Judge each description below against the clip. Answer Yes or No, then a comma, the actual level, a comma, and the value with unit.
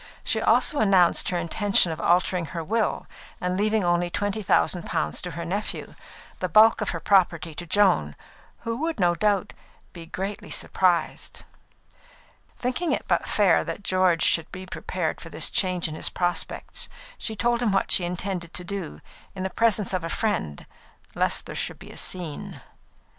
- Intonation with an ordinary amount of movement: Yes, average, 3.1 semitones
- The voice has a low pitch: No, medium, 185 Hz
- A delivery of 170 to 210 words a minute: Yes, average, 175 wpm